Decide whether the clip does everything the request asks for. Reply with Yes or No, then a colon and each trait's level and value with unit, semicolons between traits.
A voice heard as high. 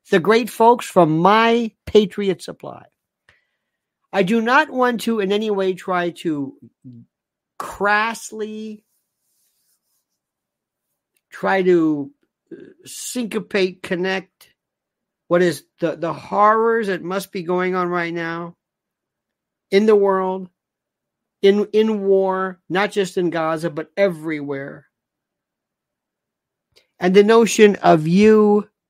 Yes: high, 195 Hz